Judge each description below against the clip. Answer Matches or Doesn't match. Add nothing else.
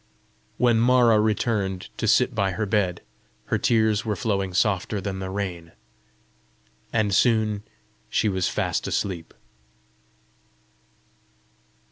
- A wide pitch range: Doesn't match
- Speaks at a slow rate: Matches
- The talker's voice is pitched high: Doesn't match